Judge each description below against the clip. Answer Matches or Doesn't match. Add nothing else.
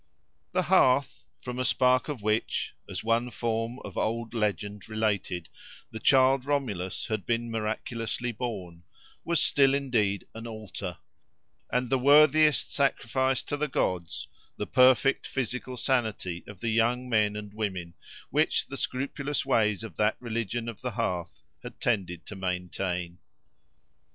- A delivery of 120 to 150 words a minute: Matches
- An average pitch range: Matches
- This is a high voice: Doesn't match